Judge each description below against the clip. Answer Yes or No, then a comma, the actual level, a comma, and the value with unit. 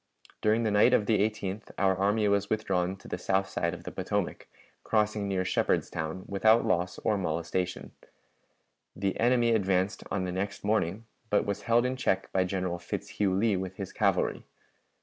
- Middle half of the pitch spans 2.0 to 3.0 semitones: Yes, narrow, 2.6 semitones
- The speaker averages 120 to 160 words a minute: No, average, 170 wpm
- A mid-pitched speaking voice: No, low, 100 Hz